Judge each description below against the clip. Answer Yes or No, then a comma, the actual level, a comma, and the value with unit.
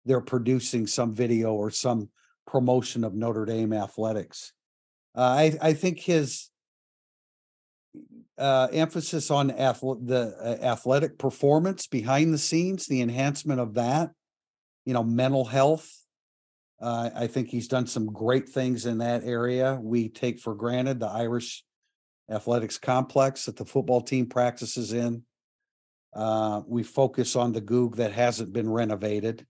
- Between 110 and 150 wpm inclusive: Yes, average, 140 wpm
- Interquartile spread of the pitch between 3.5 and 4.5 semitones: No, narrow, 2.5 semitones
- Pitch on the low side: Yes, low, 125 Hz